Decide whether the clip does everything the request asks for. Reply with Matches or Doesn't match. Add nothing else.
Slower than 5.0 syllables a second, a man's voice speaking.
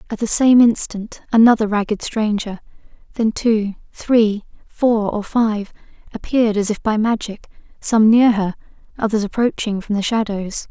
Doesn't match